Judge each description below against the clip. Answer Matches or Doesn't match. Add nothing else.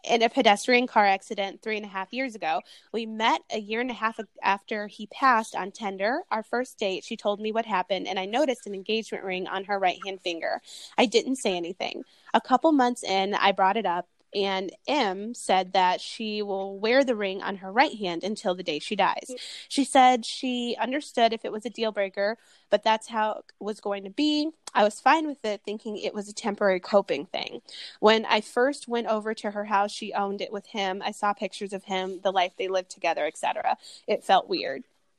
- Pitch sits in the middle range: Doesn't match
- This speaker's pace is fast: Matches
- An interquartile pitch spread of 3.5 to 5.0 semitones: Doesn't match